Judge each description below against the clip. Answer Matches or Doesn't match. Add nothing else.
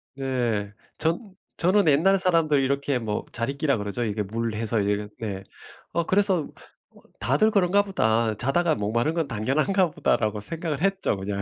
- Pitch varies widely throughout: Matches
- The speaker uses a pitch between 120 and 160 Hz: Matches